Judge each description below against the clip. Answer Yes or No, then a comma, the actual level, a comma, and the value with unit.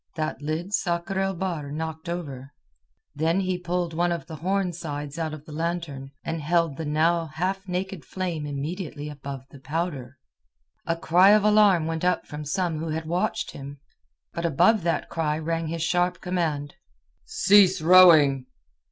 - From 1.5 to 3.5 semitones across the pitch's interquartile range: Yes, average, 3.0 semitones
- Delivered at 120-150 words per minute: No, average, 165 wpm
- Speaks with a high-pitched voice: No, medium, 165 Hz